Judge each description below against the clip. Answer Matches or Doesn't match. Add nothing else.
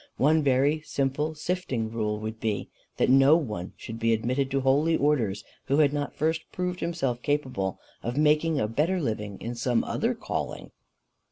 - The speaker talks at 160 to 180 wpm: Matches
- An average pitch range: Matches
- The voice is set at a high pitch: Doesn't match